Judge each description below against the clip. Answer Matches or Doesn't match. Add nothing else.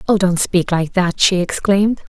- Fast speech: Doesn't match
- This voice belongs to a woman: Matches